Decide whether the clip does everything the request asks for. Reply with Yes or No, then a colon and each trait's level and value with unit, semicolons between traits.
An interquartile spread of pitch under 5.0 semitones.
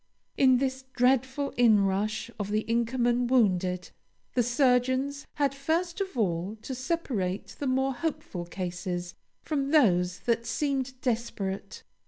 No: average, 5.3 semitones